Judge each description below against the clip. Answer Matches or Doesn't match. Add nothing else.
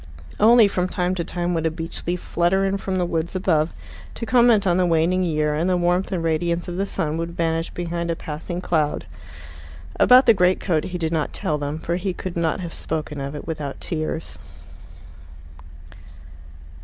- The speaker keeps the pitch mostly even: Matches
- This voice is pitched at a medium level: Matches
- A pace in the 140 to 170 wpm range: Doesn't match